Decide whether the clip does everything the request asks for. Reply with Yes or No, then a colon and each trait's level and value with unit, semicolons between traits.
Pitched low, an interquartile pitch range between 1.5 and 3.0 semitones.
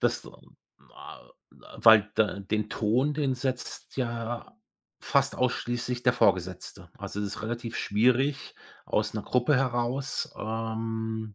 Yes: low, 115 Hz; narrow, 2.6 semitones